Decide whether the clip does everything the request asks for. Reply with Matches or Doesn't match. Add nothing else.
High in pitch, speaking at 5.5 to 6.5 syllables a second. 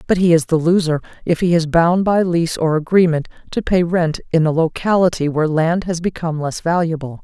Doesn't match